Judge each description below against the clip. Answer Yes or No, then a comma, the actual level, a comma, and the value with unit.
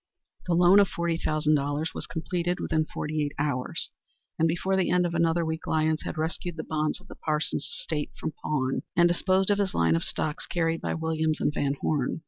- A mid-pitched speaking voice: Yes, medium, 160 Hz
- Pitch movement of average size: No, narrow, 2.2 semitones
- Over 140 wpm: Yes, average, 200 wpm